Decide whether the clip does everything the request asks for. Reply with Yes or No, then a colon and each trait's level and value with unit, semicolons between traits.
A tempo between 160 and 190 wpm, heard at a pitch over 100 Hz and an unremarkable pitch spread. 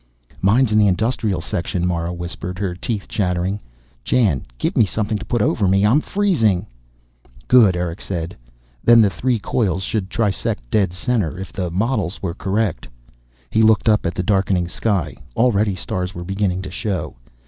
No: average, 170 wpm; very low, 95 Hz; average, 3.5 semitones